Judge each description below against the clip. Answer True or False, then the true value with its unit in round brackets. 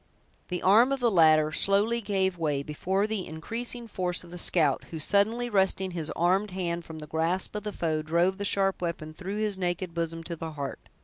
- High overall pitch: False (180 Hz)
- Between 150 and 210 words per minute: True (205 wpm)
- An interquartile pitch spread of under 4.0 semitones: True (3.6 semitones)